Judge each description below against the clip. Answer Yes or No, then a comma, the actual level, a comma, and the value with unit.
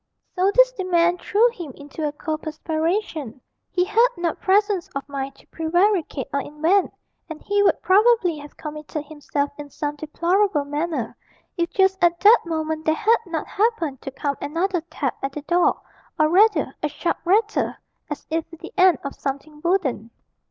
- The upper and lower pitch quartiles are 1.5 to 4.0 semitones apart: No, average, 4.4 semitones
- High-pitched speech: Yes, very high, 330 Hz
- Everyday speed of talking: Yes, average, 175 wpm